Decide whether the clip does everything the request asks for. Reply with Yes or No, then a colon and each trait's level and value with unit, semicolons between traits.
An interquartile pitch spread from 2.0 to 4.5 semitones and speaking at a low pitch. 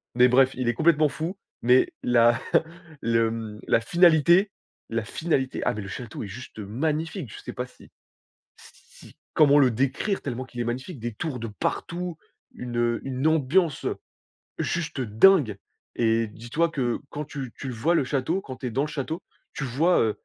No: average, 5.1 semitones; low, 130 Hz